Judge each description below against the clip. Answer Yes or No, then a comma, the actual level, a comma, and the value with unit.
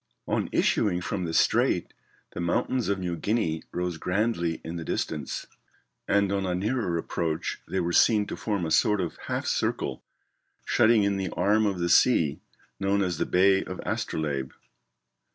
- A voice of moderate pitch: No, very low, 95 Hz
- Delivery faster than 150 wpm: Yes, average, 170 wpm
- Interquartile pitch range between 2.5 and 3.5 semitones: Yes, average, 3.1 semitones